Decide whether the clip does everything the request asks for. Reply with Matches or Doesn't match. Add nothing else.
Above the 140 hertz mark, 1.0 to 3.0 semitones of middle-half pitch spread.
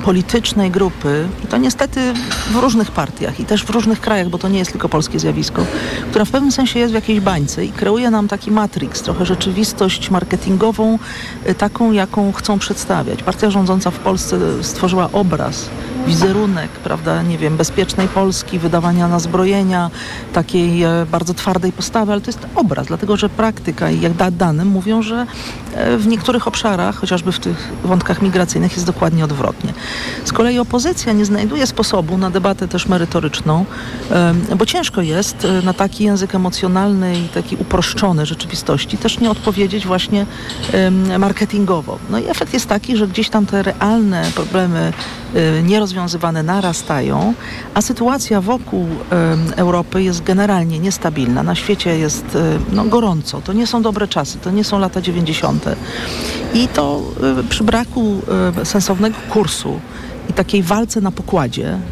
Doesn't match